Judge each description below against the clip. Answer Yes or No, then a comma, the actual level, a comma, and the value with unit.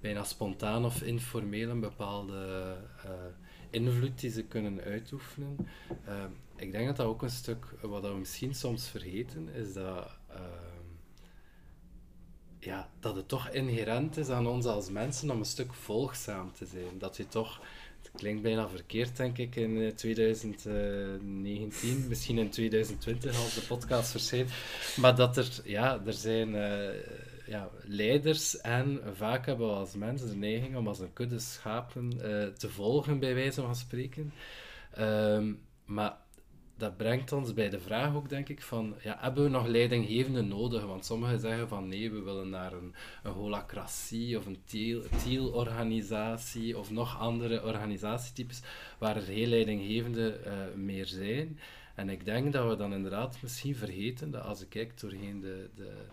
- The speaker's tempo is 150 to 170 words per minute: Yes, average, 160 wpm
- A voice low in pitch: Yes, low, 115 Hz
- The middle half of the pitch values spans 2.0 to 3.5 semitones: Yes, average, 3.1 semitones